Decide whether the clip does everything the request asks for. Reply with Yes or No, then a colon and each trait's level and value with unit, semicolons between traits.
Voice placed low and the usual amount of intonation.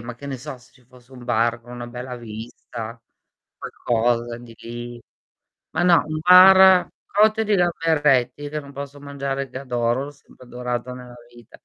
Yes: low, 125 Hz; average, 3.4 semitones